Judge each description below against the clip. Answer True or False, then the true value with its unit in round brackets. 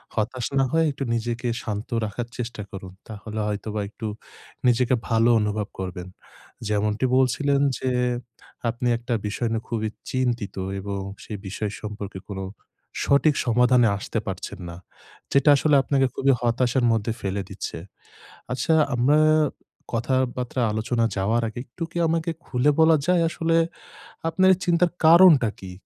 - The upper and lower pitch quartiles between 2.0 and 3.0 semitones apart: False (4.1 semitones)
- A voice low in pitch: True (120 Hz)